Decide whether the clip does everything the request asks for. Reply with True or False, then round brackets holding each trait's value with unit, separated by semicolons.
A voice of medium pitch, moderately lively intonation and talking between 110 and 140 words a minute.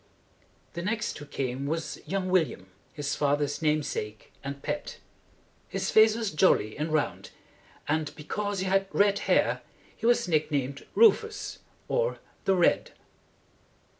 False (160 Hz; 5.9 semitones; 135 wpm)